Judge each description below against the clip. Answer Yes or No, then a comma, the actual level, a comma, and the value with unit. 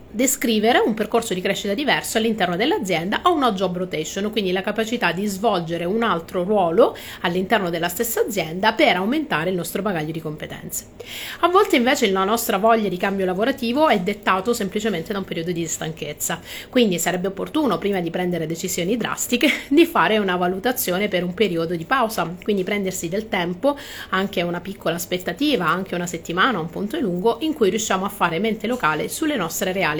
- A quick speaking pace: Yes, fast, 180 wpm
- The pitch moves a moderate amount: Yes, average, 4.5 semitones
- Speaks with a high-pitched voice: Yes, high, 200 Hz